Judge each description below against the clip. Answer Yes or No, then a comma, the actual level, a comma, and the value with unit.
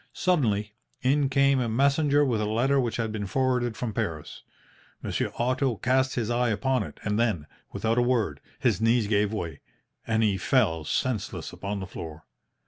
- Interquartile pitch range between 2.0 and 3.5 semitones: No, average, 3.9 semitones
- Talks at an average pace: Yes, average, 175 wpm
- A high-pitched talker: No, low, 115 Hz